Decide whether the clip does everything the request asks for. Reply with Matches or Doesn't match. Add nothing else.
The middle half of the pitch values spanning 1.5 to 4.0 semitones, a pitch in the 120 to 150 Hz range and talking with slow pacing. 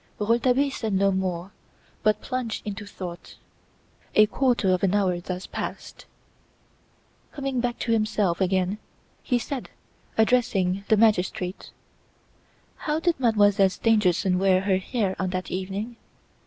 Doesn't match